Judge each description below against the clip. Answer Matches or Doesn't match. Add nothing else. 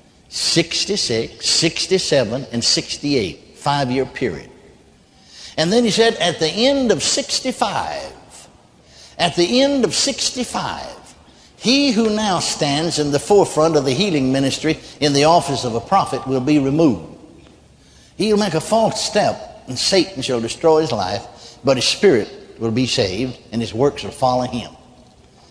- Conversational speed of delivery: Matches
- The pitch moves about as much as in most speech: Doesn't match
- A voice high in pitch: Doesn't match